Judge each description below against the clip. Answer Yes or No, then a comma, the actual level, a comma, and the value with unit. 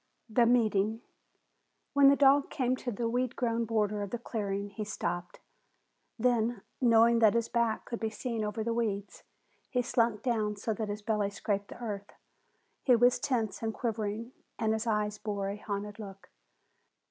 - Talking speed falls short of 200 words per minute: Yes, average, 170 wpm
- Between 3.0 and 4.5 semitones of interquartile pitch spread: No, narrow, 2.4 semitones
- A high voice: Yes, high, 220 Hz